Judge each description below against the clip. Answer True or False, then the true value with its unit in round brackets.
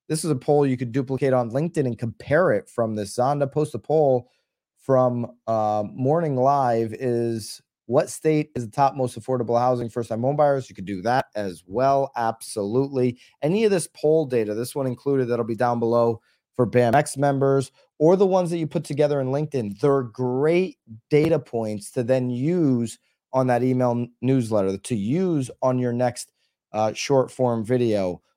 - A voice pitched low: True (130 Hz)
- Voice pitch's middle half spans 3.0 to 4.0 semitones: True (3.3 semitones)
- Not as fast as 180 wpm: False (185 wpm)